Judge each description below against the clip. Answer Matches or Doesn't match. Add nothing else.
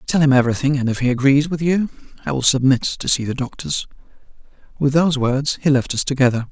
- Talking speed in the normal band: Doesn't match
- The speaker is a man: Matches